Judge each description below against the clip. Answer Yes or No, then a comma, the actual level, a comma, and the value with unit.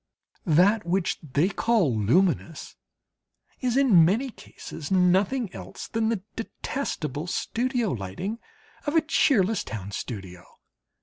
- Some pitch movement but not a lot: No, wide, 7.5 semitones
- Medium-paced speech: No, slow, 115 wpm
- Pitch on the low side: No, medium, 185 Hz